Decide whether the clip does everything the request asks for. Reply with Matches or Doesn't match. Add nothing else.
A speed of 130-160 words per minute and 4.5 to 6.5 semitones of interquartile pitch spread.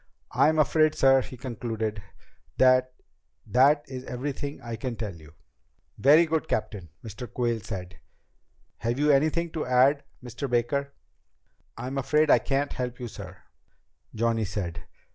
Doesn't match